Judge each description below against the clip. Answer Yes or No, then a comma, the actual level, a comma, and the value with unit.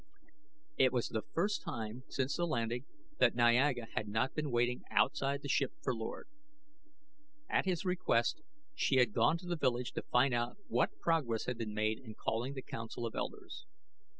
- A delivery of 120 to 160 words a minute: No, average, 175 wpm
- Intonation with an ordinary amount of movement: Yes, average, 3.9 semitones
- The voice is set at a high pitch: No, low, 125 Hz